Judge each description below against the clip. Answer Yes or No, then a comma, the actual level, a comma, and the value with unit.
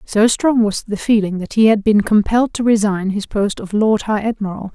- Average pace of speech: No, fast, 230 wpm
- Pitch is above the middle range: Yes, high, 210 Hz